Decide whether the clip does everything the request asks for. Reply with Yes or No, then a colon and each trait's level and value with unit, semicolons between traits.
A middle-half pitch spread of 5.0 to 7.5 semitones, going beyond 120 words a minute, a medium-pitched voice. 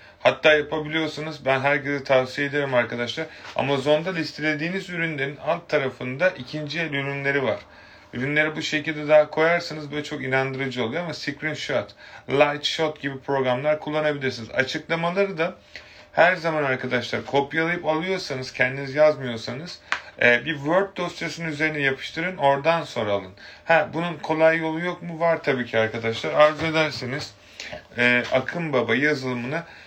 No: average, 3.3 semitones; average, 130 wpm; medium, 150 Hz